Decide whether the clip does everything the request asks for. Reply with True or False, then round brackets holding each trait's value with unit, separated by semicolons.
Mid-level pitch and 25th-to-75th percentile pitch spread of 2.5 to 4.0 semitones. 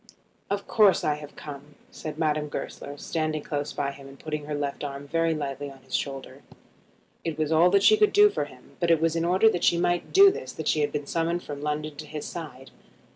True (155 Hz; 2.8 semitones)